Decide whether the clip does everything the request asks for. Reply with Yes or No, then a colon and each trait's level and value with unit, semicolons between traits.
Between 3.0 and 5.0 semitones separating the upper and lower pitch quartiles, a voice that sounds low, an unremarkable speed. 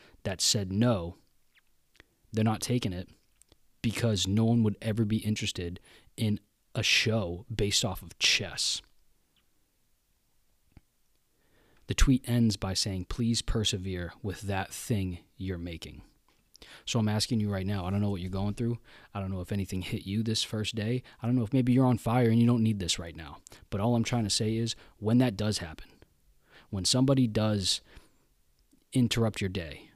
Yes: average, 3.4 semitones; low, 105 Hz; average, 175 wpm